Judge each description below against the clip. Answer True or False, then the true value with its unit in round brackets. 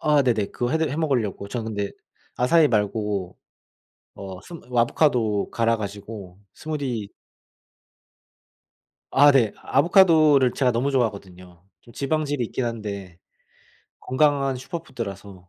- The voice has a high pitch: False (120 Hz)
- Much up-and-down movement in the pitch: True (5.8 semitones)